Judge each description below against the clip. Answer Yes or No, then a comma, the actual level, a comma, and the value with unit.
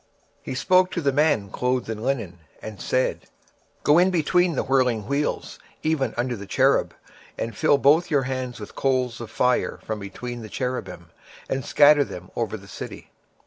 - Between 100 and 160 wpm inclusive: No, average, 175 wpm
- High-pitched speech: No, low, 130 Hz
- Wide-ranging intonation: No, average, 4.3 semitones